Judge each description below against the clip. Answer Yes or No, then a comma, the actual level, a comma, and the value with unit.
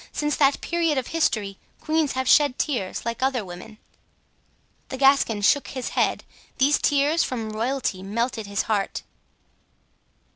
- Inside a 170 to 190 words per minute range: No, average, 140 wpm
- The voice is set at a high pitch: Yes, very high, 260 Hz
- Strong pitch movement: No, average, 4.8 semitones